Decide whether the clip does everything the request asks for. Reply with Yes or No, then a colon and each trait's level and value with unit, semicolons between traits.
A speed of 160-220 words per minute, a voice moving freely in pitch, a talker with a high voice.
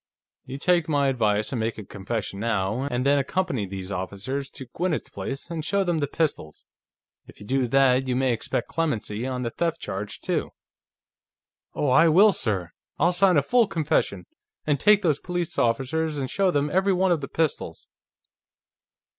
No: average, 180 wpm; wide, 6.2 semitones; low, 135 Hz